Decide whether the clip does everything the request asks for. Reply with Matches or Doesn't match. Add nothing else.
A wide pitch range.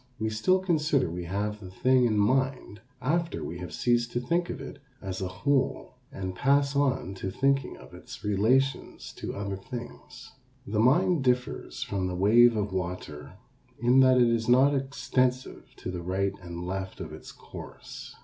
Matches